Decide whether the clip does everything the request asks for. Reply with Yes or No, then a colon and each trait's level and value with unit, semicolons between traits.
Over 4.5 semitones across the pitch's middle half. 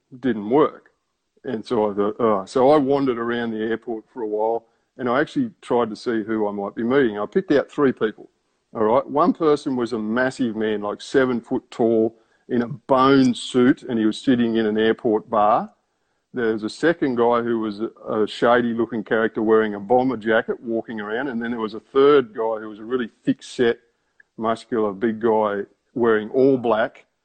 No: narrow, 2.4 semitones